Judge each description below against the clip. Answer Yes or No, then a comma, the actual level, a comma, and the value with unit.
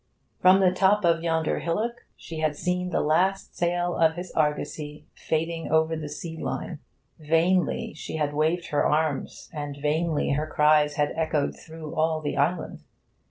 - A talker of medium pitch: Yes, medium, 160 Hz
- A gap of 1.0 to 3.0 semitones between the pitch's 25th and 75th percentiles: Yes, narrow, 2.5 semitones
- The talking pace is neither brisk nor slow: Yes, average, 160 wpm